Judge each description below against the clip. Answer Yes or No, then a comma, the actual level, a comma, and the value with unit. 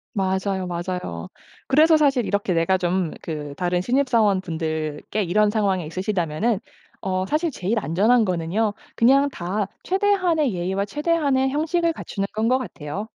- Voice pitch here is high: Yes, high, 200 Hz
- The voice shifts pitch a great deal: Yes, wide, 6.6 semitones